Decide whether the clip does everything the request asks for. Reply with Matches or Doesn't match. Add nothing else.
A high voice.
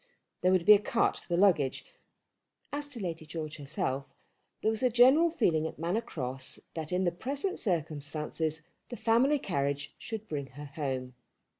Doesn't match